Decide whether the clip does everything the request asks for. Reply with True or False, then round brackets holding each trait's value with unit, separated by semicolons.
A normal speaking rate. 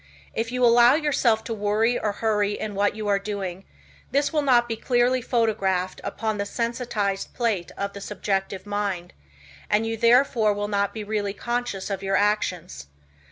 True (170 wpm)